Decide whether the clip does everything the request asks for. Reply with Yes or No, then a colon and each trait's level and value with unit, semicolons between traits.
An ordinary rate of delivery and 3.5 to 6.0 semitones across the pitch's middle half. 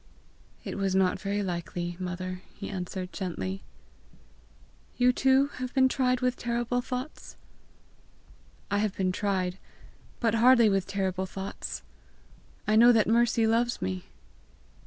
No: slow, 130 wpm; average, 4.7 semitones